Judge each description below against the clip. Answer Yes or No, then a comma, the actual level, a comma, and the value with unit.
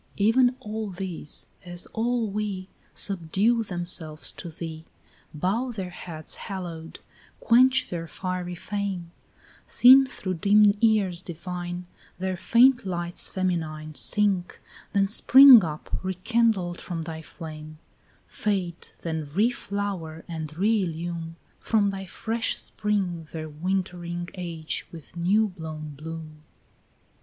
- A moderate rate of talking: No, slow, 115 wpm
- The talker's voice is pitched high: No, medium, 180 Hz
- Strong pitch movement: No, average, 4.0 semitones